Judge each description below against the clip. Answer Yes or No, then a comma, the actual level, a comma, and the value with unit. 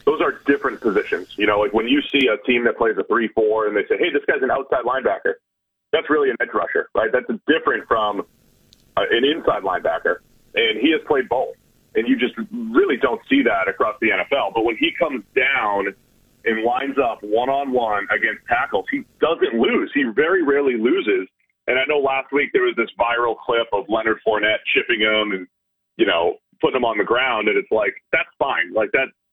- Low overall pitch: No, very high, 350 Hz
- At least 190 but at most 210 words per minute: Yes, fast, 205 wpm